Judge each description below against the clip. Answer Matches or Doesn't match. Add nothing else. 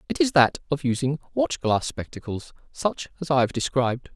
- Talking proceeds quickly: Doesn't match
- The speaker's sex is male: Matches